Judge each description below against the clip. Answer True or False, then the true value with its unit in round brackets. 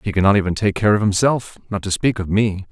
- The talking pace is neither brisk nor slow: False (290 wpm)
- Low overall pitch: True (100 Hz)